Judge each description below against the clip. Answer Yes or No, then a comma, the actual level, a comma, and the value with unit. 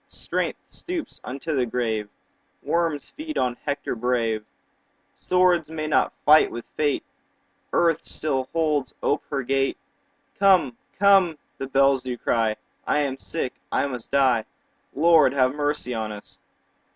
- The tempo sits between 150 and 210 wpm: No, average, 140 wpm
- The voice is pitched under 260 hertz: Yes, medium, 140 Hz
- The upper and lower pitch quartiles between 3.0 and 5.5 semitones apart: Yes, average, 4.3 semitones